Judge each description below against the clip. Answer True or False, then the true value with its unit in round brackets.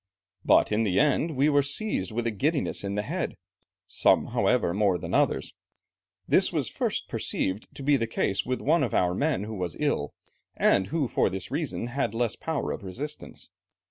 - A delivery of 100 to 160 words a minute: False (190 wpm)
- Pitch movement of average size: False (6.6 semitones)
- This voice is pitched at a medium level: False (120 Hz)